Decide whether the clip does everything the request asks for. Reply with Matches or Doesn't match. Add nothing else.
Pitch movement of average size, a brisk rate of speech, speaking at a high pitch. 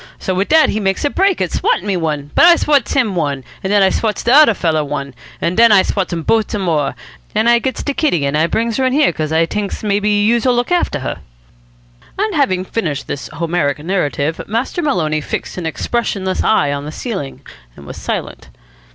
Doesn't match